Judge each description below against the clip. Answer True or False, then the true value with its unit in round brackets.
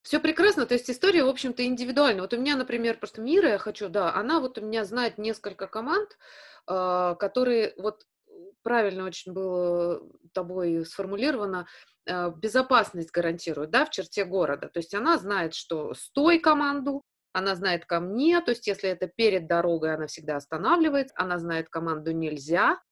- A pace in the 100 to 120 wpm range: False (160 wpm)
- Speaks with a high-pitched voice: True (205 Hz)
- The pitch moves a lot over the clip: True (6.5 semitones)